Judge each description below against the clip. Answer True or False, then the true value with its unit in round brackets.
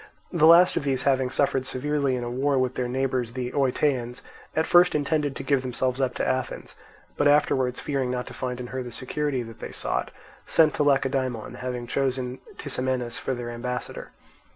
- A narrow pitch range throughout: True (2.1 semitones)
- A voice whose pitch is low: True (130 Hz)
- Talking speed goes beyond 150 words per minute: True (190 wpm)